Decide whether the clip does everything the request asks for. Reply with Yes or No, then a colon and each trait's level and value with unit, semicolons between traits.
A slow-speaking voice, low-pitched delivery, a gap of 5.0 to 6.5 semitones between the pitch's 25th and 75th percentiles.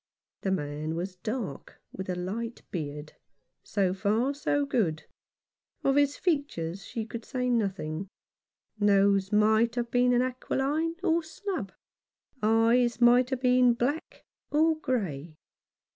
No: slow, 125 wpm; high, 230 Hz; average, 5.3 semitones